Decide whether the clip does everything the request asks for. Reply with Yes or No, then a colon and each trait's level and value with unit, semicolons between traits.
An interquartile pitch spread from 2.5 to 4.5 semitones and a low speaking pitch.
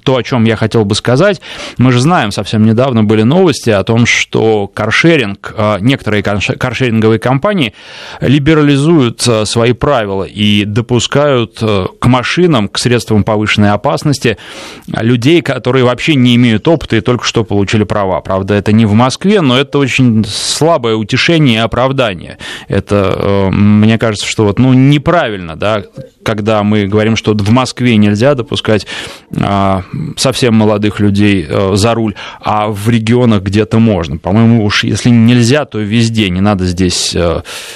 Yes: average, 3.4 semitones; low, 115 Hz